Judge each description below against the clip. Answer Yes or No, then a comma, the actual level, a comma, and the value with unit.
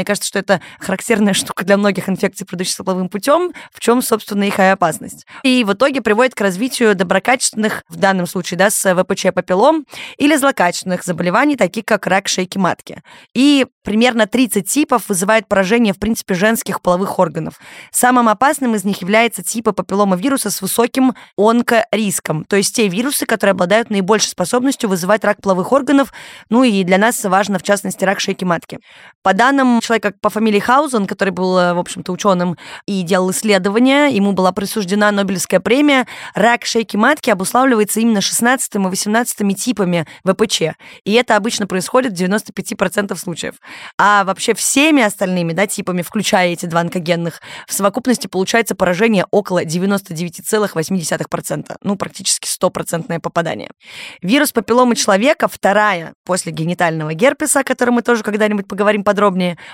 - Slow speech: No, average, 155 wpm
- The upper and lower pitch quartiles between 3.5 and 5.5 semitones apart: Yes, average, 3.8 semitones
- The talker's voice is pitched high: Yes, high, 205 Hz